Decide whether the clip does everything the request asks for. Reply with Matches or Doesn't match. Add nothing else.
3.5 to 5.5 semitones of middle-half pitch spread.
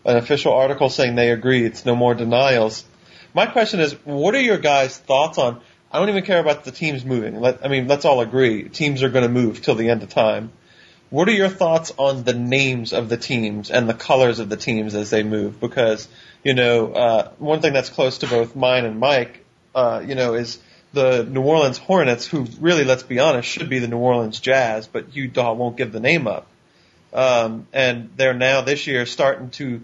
Doesn't match